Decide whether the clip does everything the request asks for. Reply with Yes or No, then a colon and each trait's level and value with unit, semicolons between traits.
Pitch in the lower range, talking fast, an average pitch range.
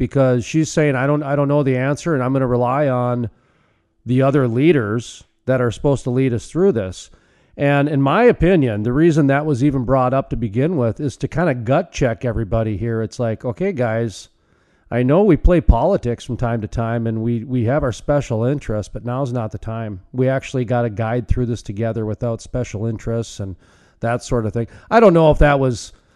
Yes: low, 125 Hz; fast, 220 wpm; average, 3.6 semitones